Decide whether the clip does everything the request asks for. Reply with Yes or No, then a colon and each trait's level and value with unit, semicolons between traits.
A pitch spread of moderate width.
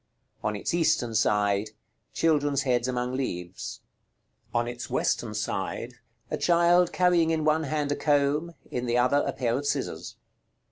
Yes: average, 4.7 semitones